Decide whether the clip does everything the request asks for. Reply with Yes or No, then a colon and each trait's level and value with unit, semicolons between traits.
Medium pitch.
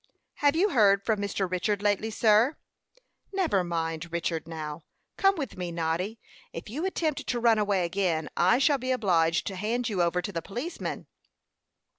No: high, 200 Hz